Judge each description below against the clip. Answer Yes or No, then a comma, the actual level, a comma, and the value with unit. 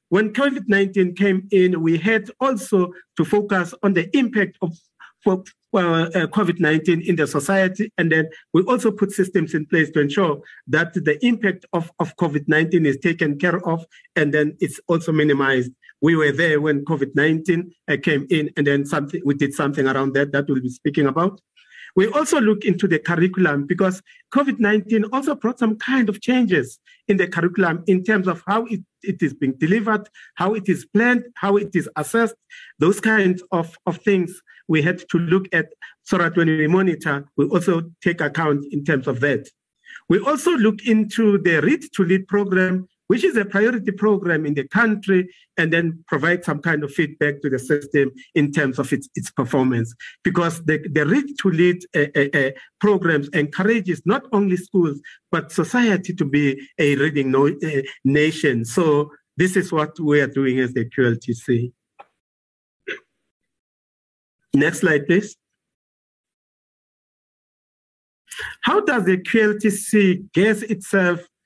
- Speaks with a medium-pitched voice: Yes, medium, 175 Hz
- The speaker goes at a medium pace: Yes, average, 165 wpm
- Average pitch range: Yes, average, 4.9 semitones